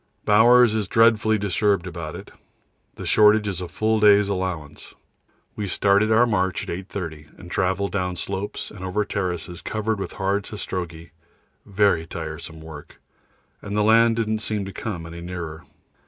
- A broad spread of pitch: No, average, 3.4 semitones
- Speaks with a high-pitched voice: No, low, 100 Hz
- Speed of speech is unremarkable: Yes, average, 155 wpm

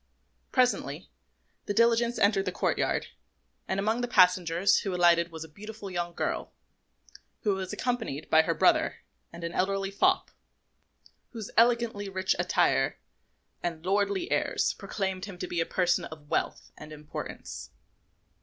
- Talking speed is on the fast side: No, average, 145 wpm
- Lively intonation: No, average, 3.6 semitones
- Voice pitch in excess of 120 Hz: Yes, high, 190 Hz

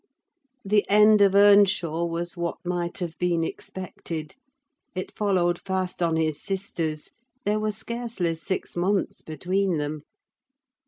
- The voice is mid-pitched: Yes, medium, 180 Hz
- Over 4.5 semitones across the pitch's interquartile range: No, average, 3.2 semitones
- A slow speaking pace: Yes, slow, 125 wpm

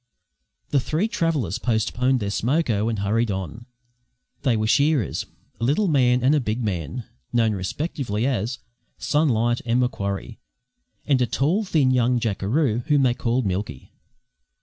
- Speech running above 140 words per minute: Yes, average, 150 wpm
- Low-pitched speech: Yes, low, 120 Hz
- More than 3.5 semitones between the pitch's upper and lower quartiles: Yes, average, 4.4 semitones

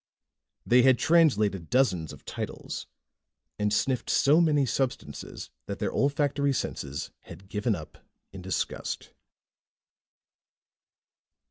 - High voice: No, low, 125 Hz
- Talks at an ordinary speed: No, slow, 105 wpm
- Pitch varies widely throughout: Yes, wide, 6.1 semitones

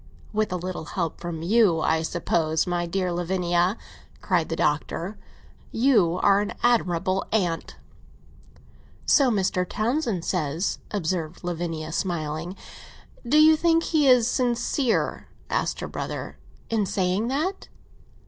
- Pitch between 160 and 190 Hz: Yes, medium, 185 Hz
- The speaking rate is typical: No, slow, 125 wpm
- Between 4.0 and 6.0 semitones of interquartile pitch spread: Yes, average, 5.1 semitones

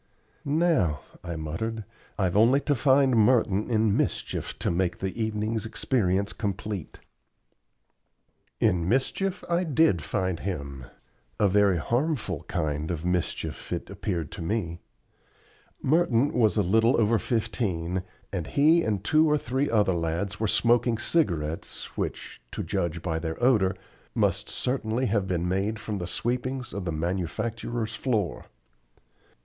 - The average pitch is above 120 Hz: No, low, 105 Hz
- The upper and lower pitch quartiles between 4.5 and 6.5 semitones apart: Yes, wide, 5.4 semitones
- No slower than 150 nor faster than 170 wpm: No, slow, 135 wpm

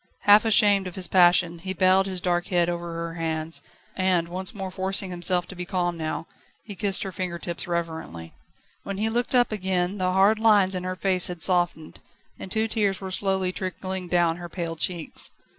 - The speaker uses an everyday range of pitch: No, narrow, 1.9 semitones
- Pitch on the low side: No, medium, 185 Hz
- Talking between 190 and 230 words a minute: Yes, average, 195 wpm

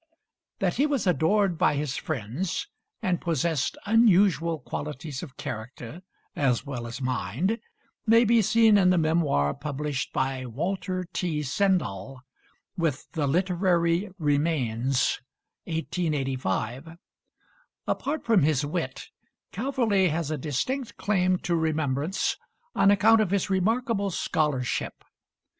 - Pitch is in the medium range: Yes, medium, 165 Hz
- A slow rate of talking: Yes, slow, 115 wpm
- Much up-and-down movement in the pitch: Yes, wide, 6.0 semitones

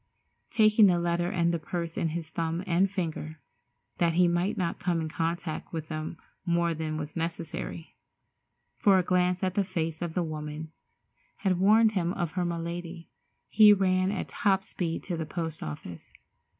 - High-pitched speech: No, medium, 170 Hz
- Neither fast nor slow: Yes, average, 165 wpm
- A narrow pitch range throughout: Yes, narrow, 2.2 semitones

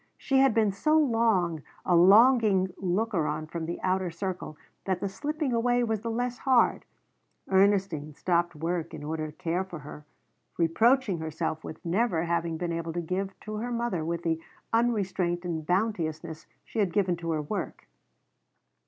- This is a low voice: No, medium, 185 Hz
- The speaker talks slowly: No, average, 170 wpm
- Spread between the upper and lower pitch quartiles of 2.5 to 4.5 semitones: No, average, 5.1 semitones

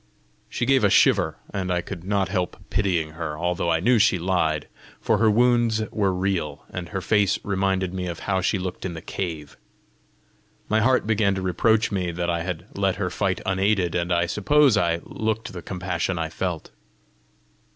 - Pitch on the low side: Yes, very low, 95 Hz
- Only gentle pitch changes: No, average, 3.1 semitones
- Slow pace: No, average, 185 wpm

